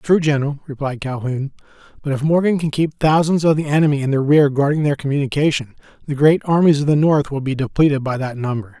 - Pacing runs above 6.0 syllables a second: Yes, 6.2 syllables/s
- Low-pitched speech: No, medium, 145 Hz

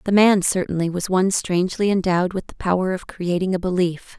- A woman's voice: Yes, female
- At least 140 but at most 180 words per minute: No, average, 200 wpm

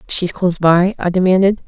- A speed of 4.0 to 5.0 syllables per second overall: No, 5.5 syllables/s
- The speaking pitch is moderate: Yes, medium, 180 Hz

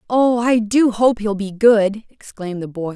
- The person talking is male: No, female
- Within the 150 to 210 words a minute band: Yes, fast, 205 wpm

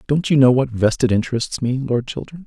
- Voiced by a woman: No, male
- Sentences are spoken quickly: Yes, fast, 220 wpm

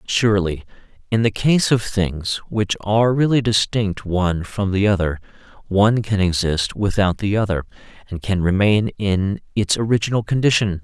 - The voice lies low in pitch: Yes, low, 100 Hz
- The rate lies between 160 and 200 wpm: No, average, 150 wpm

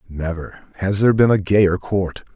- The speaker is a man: Yes, male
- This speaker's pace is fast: No, average, 180 wpm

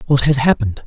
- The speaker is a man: Yes, male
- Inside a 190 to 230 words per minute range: Yes, fast, 210 wpm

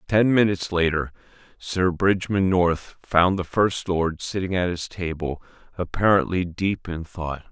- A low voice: Yes, very low, 90 Hz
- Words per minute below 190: Yes, average, 145 wpm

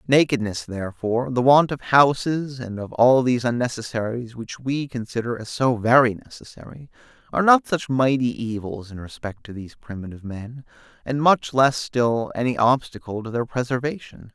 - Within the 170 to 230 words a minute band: No, average, 160 wpm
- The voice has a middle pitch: No, low, 125 Hz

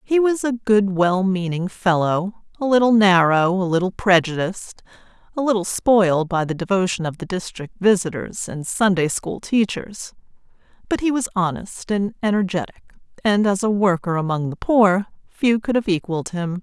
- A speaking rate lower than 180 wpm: Yes, average, 160 wpm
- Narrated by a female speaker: Yes, female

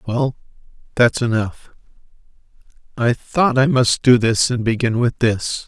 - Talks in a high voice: No, low, 120 Hz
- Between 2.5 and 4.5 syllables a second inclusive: Yes, 4.1 syllables/s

